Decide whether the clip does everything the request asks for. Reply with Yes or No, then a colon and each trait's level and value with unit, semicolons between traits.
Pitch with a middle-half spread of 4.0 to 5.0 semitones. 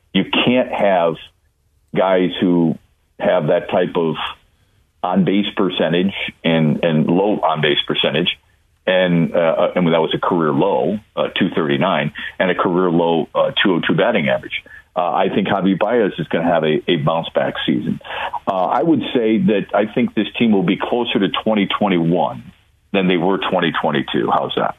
No: average, 2.7 semitones